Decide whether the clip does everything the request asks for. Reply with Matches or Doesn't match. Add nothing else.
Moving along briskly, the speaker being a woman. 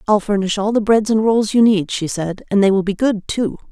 Matches